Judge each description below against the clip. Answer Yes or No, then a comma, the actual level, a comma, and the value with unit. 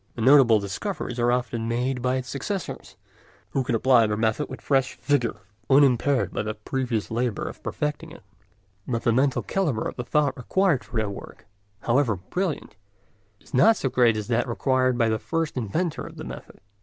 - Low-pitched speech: Yes, low, 125 Hz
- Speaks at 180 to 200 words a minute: Yes, average, 185 wpm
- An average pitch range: Yes, average, 3.6 semitones